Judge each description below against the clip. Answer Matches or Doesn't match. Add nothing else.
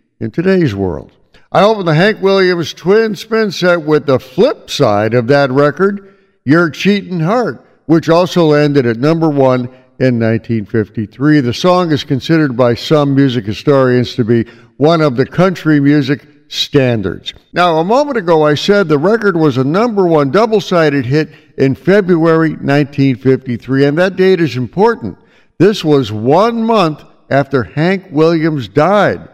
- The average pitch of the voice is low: Doesn't match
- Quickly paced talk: Doesn't match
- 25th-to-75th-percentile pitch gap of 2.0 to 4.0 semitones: Doesn't match